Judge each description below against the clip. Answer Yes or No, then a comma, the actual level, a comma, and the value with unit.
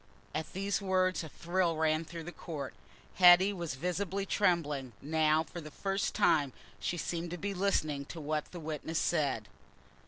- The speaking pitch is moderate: Yes, medium, 165 Hz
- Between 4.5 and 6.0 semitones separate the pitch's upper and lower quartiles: No, average, 3.1 semitones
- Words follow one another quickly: No, average, 165 wpm